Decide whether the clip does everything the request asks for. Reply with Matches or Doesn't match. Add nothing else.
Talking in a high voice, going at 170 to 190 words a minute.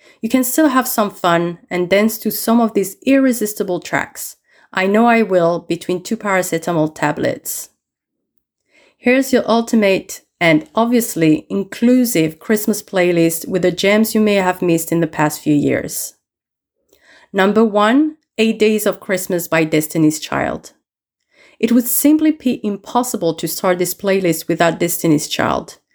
Doesn't match